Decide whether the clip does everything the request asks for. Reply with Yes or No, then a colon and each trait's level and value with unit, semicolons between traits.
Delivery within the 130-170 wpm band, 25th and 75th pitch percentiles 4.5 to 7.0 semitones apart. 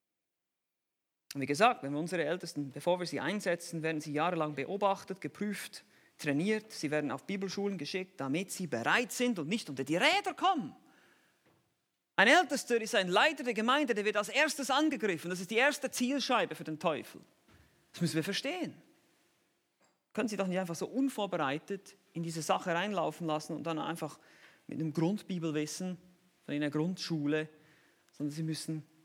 Yes: average, 165 wpm; average, 5.3 semitones